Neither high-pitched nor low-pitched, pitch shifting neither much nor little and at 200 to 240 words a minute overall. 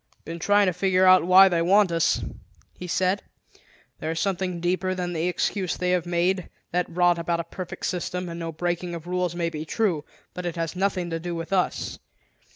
No: medium, 175 Hz; narrow, 1.5 semitones; fast, 205 wpm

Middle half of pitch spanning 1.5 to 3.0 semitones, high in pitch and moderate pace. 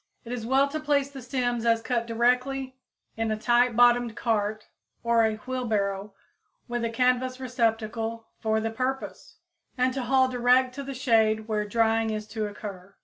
Yes: narrow, 2.4 semitones; high, 235 Hz; average, 170 wpm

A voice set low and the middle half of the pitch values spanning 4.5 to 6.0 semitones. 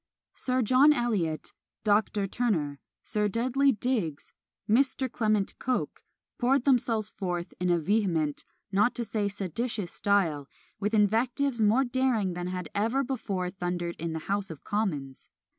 No: high, 210 Hz; average, 5.2 semitones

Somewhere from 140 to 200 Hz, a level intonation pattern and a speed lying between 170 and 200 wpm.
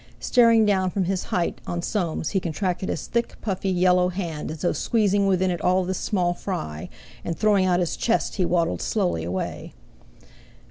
Yes: medium, 185 Hz; narrow, 2.3 semitones; average, 180 wpm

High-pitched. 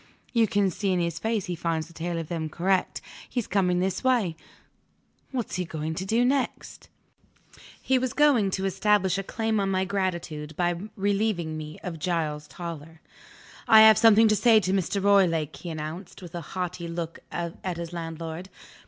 No: medium, 180 Hz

